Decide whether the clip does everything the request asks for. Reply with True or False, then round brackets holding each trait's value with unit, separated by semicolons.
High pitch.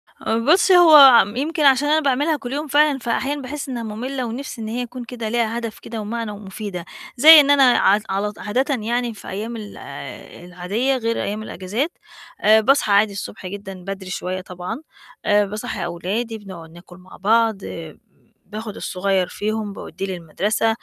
True (220 Hz)